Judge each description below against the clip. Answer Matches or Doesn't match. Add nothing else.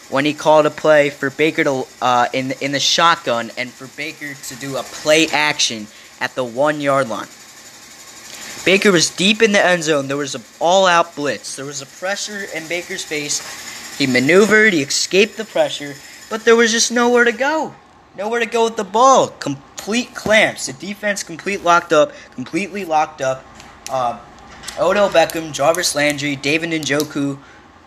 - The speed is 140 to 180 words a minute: Matches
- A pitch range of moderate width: Doesn't match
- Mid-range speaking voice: Matches